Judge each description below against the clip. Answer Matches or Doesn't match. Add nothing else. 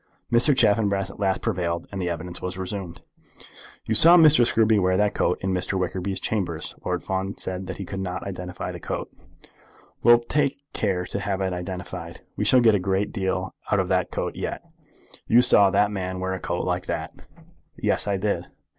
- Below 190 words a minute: Doesn't match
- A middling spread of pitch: Doesn't match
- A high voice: Doesn't match